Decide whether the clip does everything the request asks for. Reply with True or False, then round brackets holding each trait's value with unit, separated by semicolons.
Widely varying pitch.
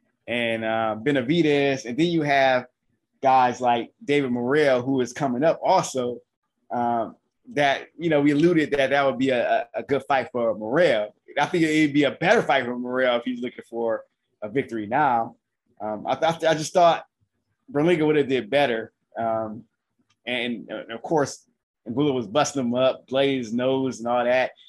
False (3.3 semitones)